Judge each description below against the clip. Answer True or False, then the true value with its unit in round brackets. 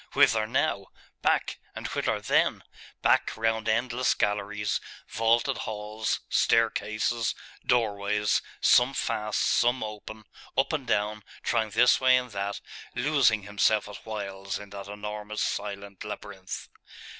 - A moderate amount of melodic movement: False (2.2 semitones)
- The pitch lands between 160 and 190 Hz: False (110 Hz)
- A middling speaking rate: False (120 wpm)